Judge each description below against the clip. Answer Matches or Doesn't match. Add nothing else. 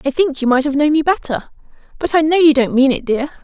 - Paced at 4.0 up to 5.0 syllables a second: Doesn't match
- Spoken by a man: Doesn't match